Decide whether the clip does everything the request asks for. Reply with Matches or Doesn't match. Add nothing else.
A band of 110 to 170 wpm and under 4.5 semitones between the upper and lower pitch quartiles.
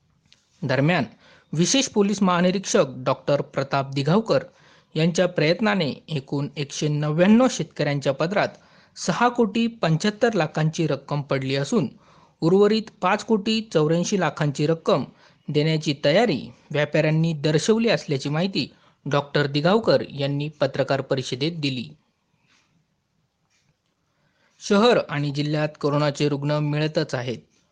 Doesn't match